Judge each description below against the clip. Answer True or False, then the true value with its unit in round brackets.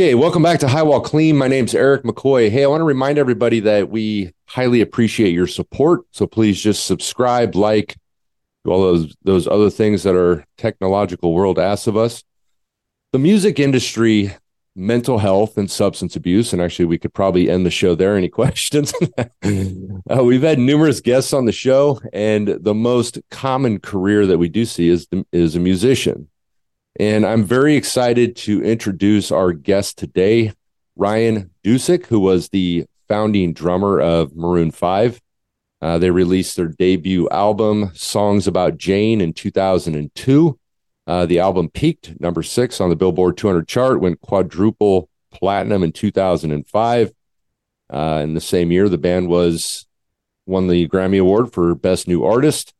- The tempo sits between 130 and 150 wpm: False (165 wpm)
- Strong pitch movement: False (4.8 semitones)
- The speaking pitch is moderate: False (100 Hz)